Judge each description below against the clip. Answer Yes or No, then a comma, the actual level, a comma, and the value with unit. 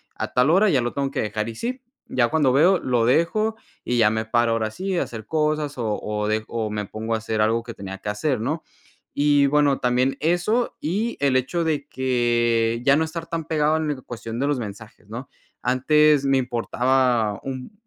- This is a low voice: Yes, low, 130 Hz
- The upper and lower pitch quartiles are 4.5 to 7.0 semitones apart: Yes, average, 4.9 semitones